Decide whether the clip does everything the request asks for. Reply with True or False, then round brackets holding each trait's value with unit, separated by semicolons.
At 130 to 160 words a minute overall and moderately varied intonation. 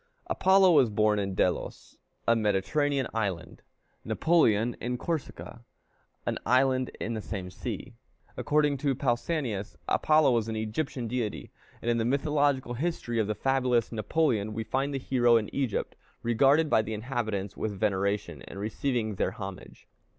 True (150 wpm; 4.2 semitones)